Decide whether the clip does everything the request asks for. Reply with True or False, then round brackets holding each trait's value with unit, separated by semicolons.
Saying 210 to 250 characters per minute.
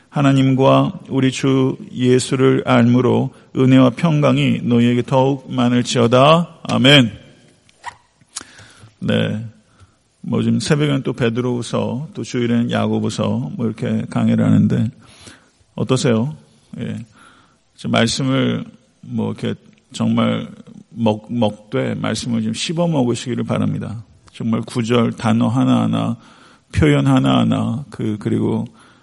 True (240 characters per minute)